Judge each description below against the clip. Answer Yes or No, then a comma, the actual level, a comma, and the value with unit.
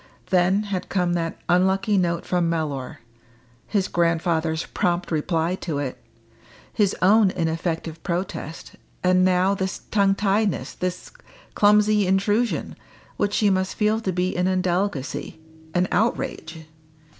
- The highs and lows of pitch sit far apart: No, average, 2.8 semitones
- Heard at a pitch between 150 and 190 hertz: Yes, medium, 185 Hz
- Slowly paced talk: Yes, slow, 125 wpm